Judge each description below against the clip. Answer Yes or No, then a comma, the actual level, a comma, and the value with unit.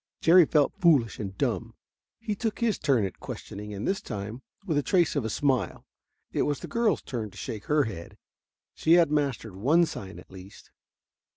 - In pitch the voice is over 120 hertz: Yes, medium, 140 Hz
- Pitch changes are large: Yes, wide, 8.1 semitones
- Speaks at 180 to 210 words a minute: Yes, average, 190 wpm